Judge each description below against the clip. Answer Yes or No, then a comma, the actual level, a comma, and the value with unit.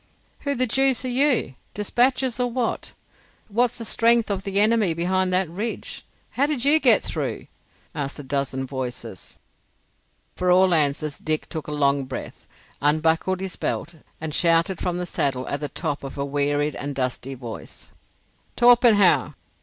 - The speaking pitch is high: No, medium, 180 Hz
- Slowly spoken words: No, average, 160 wpm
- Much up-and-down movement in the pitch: Yes, wide, 8.3 semitones